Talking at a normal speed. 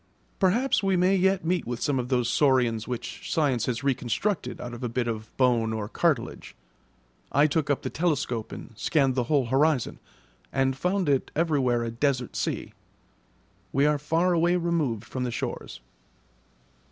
Yes: average, 165 wpm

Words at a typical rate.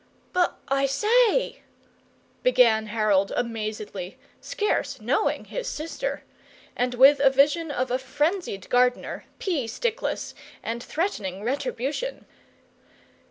No: slow, 110 wpm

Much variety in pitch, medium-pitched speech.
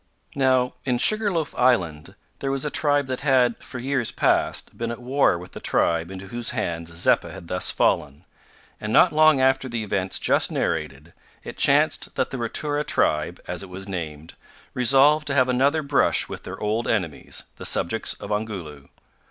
No: wide, 7.1 semitones; low, 120 Hz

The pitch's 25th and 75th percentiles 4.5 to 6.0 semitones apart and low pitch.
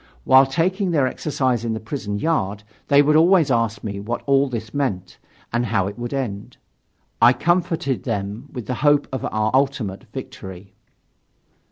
Yes: average, 5.0 semitones; low, 125 Hz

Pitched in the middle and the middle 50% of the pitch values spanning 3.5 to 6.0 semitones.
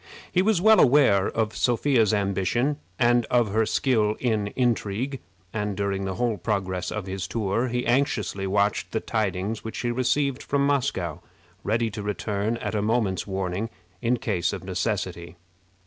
No: low, 110 Hz; average, 3.8 semitones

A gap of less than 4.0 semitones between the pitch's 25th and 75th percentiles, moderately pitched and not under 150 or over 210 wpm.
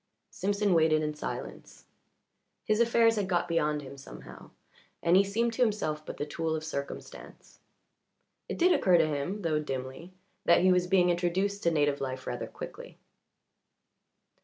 No: average, 4.8 semitones; medium, 170 Hz; average, 160 wpm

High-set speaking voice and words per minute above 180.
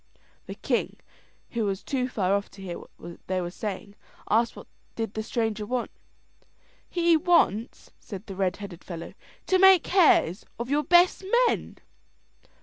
No: high, 220 Hz; average, 155 wpm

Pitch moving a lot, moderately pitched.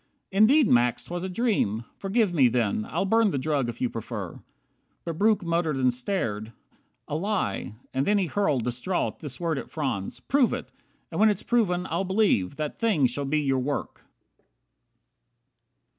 Yes: wide, 7.9 semitones; medium, 155 Hz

